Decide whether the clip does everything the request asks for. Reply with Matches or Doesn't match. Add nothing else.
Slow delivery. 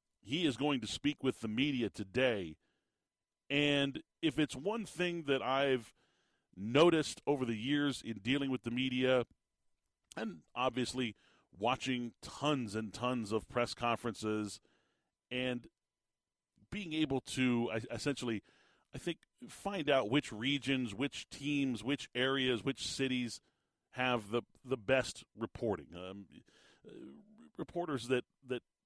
Matches